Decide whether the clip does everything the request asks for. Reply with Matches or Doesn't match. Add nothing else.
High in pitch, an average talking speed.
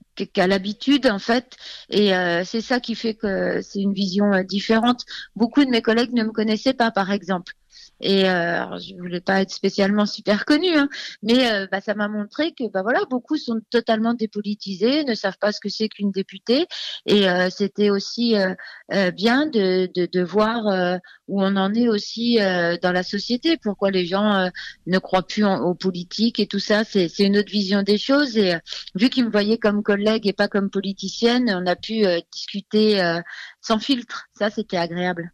Matches